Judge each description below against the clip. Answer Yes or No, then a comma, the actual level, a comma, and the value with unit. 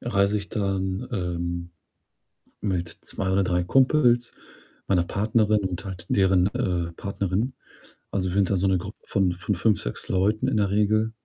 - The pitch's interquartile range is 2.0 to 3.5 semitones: Yes, average, 2.8 semitones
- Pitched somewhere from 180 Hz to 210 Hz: No, very low, 95 Hz